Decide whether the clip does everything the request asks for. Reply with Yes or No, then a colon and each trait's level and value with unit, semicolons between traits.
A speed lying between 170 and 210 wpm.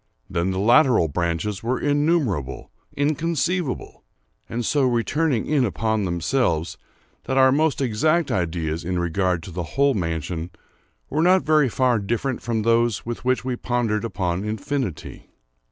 No: slow, 135 wpm